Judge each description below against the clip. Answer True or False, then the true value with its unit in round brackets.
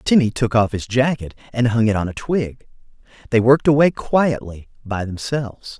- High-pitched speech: False (120 Hz)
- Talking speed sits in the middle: True (175 wpm)